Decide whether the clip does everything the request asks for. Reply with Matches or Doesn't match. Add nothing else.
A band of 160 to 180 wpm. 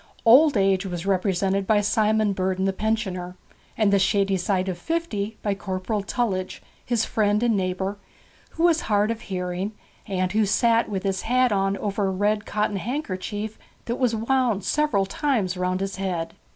Matches